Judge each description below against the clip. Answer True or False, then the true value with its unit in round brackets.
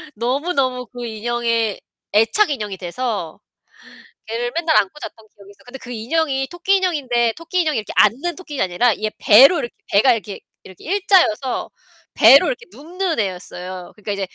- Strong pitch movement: True (6.9 semitones)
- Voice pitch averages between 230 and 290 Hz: True (240 Hz)